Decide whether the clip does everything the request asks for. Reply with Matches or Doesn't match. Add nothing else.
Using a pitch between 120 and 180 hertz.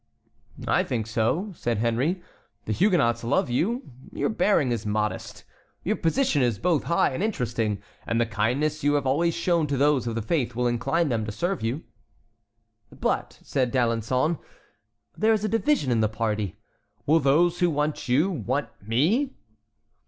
Matches